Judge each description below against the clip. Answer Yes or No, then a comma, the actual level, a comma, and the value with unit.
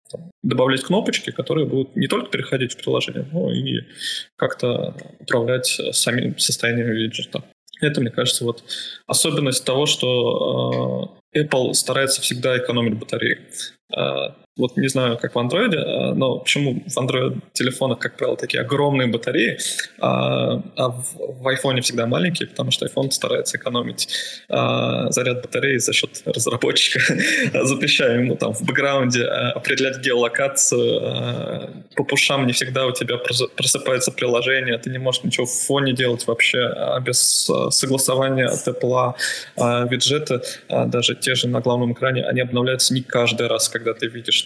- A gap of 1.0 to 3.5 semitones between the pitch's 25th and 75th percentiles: Yes, narrow, 2.4 semitones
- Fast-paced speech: No, average, 135 wpm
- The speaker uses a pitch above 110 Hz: Yes, low, 125 Hz